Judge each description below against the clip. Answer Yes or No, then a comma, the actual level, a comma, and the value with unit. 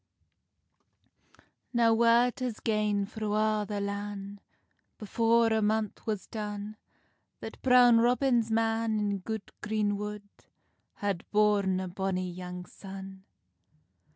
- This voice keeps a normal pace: No, slow, 115 wpm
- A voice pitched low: No, high, 210 Hz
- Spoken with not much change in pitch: Yes, narrow, 2.0 semitones